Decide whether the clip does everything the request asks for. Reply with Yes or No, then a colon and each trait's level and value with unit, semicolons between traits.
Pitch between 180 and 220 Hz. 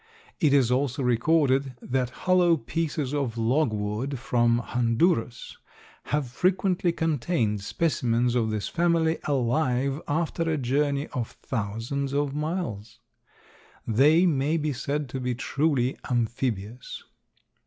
No: low, 135 Hz